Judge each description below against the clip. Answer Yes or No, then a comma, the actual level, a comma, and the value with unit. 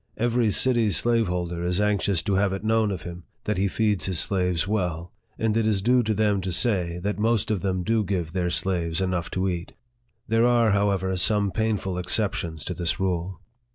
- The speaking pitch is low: Yes, very low, 95 Hz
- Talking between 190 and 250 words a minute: Yes, average, 195 wpm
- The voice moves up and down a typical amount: Yes, average, 3.4 semitones